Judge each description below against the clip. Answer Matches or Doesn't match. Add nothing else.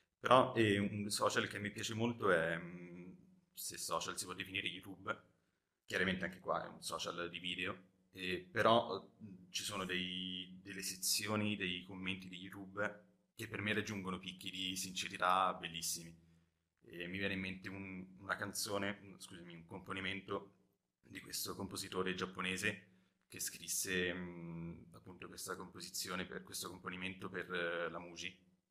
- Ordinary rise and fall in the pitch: Doesn't match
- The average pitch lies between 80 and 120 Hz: Matches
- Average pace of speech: Matches